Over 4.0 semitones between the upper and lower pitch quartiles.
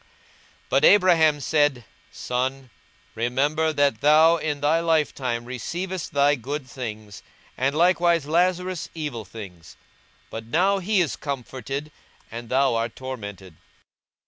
Yes: average, 4.9 semitones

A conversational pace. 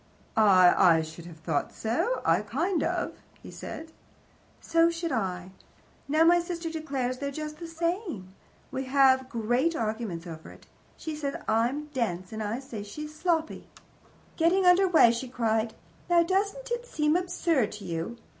Yes: average, 155 wpm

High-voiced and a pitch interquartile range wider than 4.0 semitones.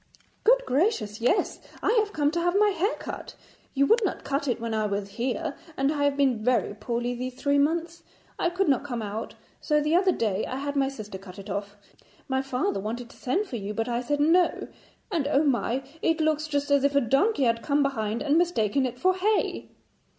Yes: very high, 275 Hz; wide, 5.6 semitones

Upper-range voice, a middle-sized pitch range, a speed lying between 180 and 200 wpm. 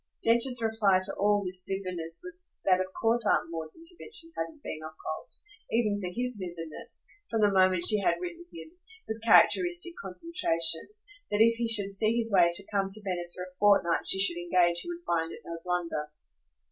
Yes: high, 200 Hz; average, 4.8 semitones; average, 190 wpm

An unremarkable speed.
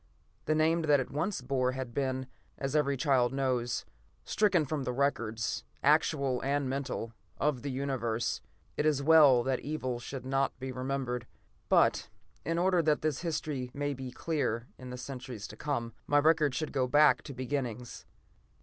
Yes: average, 165 wpm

